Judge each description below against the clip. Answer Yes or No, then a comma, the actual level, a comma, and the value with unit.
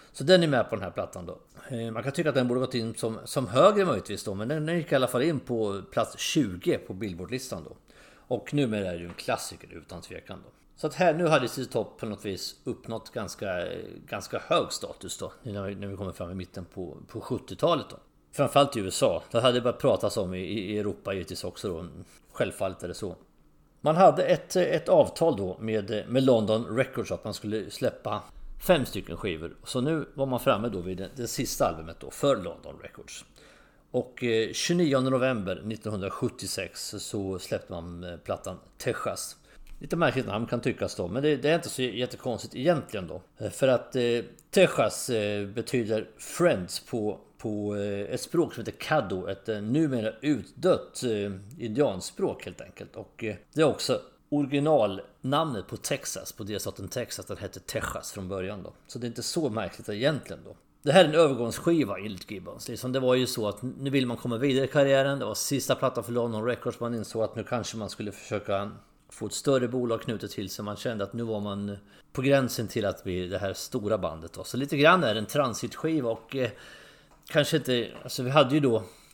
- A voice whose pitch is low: Yes, low, 115 Hz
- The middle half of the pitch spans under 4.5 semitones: No, average, 4.8 semitones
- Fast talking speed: No, average, 195 wpm